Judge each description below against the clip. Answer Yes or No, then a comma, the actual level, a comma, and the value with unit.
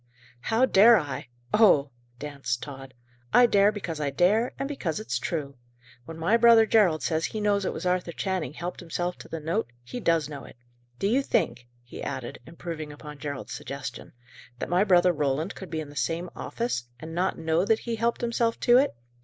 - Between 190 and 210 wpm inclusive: Yes, average, 195 wpm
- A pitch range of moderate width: No, wide, 6.1 semitones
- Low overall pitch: No, medium, 170 Hz